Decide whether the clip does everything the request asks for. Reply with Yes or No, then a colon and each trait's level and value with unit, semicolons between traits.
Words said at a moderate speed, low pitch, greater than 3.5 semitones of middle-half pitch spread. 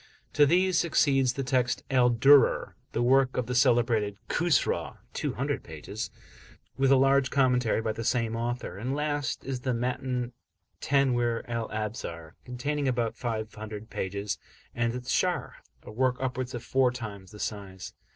No: average, 150 wpm; low, 125 Hz; average, 3.0 semitones